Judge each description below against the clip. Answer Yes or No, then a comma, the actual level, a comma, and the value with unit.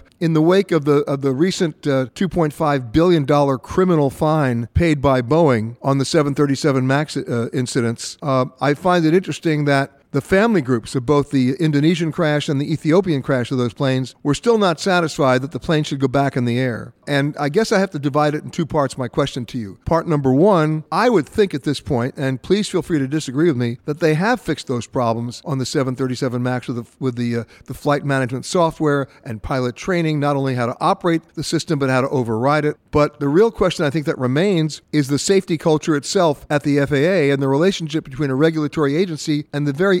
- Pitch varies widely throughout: No, average, 3.3 semitones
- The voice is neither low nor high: Yes, medium, 145 Hz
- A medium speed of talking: No, fast, 220 wpm